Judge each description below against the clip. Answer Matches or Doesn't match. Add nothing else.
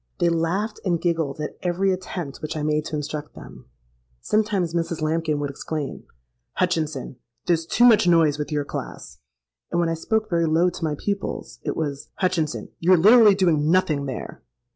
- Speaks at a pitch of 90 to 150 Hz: Doesn't match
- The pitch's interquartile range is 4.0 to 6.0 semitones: Doesn't match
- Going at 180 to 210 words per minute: Doesn't match